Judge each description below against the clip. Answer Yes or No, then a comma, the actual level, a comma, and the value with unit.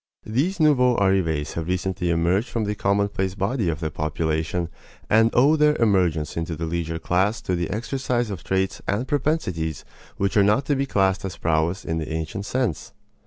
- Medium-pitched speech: No, very low, 95 Hz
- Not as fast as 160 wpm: No, average, 180 wpm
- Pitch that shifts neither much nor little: No, wide, 5.7 semitones